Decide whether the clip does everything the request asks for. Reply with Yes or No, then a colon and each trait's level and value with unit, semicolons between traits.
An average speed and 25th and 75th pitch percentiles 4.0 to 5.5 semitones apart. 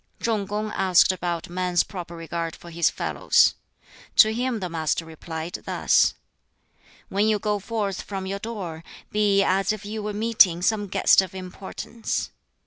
No: average, 155 wpm; average, 3.5 semitones